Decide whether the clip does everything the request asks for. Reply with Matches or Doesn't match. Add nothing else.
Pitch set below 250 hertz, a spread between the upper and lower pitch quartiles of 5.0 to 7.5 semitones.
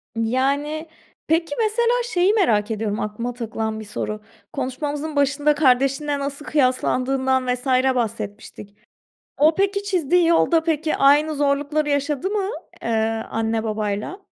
Doesn't match